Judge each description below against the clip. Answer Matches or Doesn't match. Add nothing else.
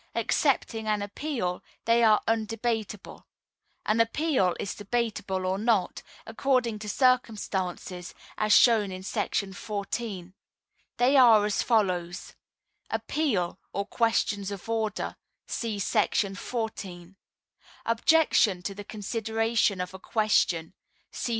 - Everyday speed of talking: Doesn't match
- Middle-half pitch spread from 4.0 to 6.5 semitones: Doesn't match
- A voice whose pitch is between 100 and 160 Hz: Doesn't match